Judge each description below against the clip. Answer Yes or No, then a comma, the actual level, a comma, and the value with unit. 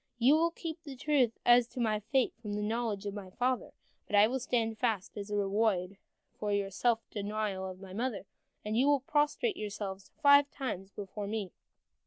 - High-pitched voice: Yes, high, 220 Hz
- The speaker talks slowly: No, average, 195 wpm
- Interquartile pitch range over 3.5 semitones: Yes, average, 4.1 semitones